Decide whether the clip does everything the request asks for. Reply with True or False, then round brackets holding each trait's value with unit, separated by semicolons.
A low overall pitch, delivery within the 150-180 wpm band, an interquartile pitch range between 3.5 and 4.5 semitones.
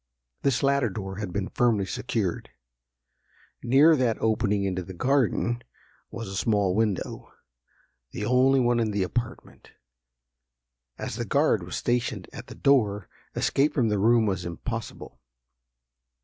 False (110 Hz; 135 wpm; 3.8 semitones)